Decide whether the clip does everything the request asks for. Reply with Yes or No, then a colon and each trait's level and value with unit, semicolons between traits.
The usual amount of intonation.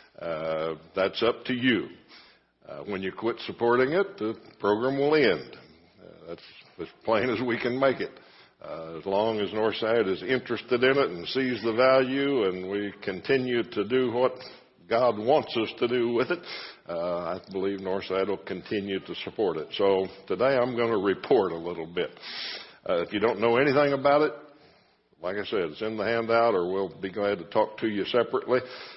Yes: average, 4.6 semitones